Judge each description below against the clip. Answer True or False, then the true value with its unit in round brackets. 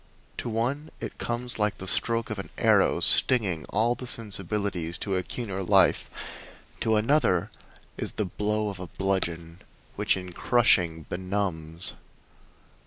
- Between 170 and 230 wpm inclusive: False (140 wpm)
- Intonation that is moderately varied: True (4.0 semitones)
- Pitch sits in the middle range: False (100 Hz)